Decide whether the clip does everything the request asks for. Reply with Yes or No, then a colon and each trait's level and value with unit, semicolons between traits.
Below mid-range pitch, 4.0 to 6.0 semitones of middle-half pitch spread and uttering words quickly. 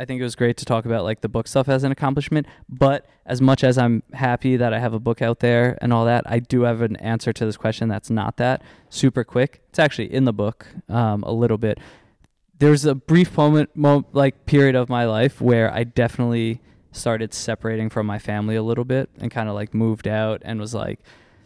No: low, 120 Hz; average, 2.9 semitones; fast, 230 wpm